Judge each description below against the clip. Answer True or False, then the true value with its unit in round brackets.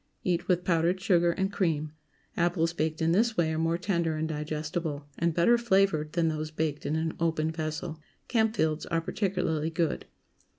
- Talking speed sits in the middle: True (170 wpm)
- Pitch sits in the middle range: True (165 Hz)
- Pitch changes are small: True (2.2 semitones)